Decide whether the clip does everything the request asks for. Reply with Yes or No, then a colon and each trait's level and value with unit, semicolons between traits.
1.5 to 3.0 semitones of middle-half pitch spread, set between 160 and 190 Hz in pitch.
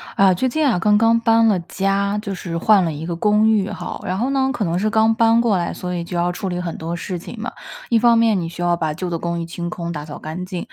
No: average, 4.3 semitones; medium, 185 Hz